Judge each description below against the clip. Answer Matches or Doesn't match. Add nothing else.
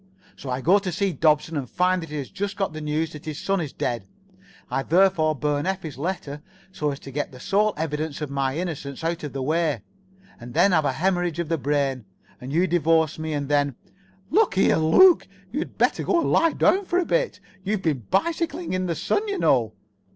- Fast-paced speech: Matches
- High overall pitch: Doesn't match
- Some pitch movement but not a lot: Matches